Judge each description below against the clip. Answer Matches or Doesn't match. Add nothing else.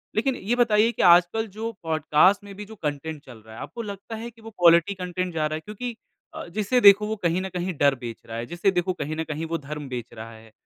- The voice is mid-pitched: Matches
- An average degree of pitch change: Doesn't match